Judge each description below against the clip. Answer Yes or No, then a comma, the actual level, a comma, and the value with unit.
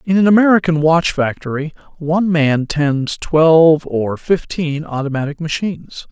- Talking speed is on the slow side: Yes, slow, 130 wpm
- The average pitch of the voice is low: No, medium, 160 Hz